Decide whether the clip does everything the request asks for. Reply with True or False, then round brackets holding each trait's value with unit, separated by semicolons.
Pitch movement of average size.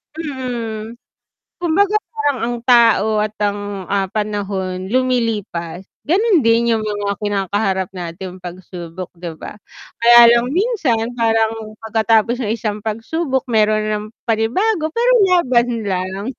True (3.6 semitones)